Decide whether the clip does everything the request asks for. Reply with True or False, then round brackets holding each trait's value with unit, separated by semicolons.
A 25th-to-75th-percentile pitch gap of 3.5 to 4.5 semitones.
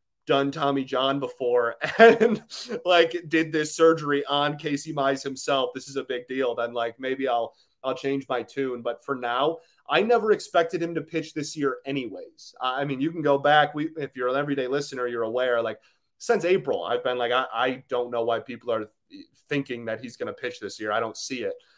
True (4.0 semitones)